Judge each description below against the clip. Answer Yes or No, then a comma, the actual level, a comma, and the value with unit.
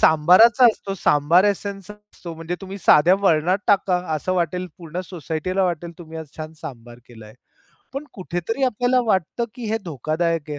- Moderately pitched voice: Yes, medium, 175 Hz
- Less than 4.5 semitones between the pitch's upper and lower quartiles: Yes, average, 4.1 semitones